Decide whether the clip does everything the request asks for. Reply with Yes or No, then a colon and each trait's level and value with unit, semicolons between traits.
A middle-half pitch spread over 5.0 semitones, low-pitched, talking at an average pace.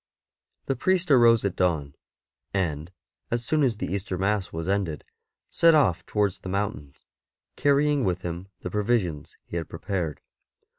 Yes: wide, 5.6 semitones; low, 100 Hz; average, 160 wpm